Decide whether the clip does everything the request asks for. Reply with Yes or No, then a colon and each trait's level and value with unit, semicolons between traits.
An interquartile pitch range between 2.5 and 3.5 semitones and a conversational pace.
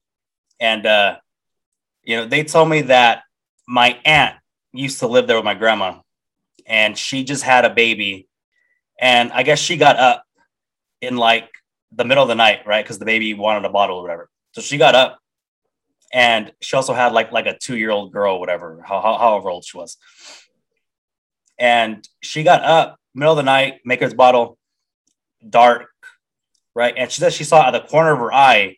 No: average, 5.3 semitones; average, 190 wpm